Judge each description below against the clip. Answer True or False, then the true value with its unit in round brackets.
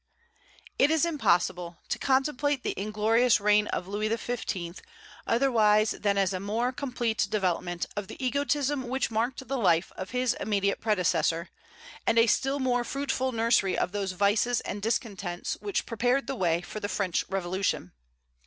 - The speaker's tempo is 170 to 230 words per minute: False (155 wpm)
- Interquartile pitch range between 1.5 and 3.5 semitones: False (4.6 semitones)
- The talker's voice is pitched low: False (215 Hz)